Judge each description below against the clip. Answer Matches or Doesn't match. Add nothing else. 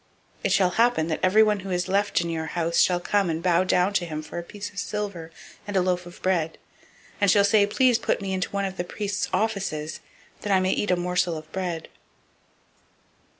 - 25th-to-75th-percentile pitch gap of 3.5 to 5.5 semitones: Doesn't match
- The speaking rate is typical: Doesn't match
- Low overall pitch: Doesn't match